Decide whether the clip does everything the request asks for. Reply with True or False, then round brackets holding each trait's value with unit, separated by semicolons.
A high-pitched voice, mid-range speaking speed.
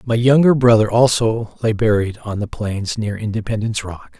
False (110 Hz; 170 wpm)